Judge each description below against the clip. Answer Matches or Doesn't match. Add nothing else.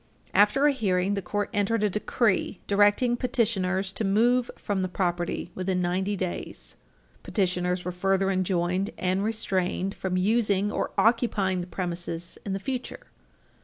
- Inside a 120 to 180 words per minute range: Matches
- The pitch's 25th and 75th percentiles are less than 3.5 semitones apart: Matches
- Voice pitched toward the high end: Matches